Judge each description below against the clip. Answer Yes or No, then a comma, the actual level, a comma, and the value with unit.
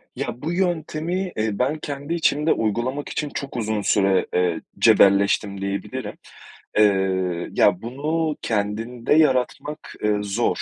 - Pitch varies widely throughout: Yes, wide, 6.9 semitones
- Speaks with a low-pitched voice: Yes, low, 120 Hz